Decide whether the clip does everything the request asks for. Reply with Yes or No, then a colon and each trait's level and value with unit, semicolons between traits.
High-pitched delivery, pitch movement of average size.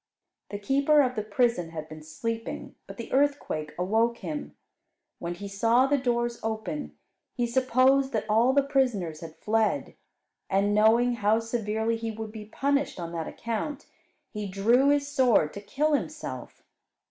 Yes: high, 225 Hz; average, 4.4 semitones